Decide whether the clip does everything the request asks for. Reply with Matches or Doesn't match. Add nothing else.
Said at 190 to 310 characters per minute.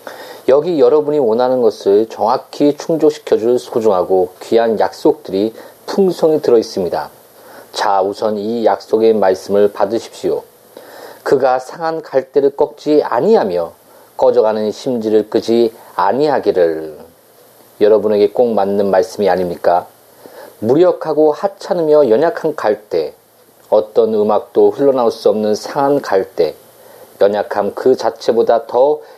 Matches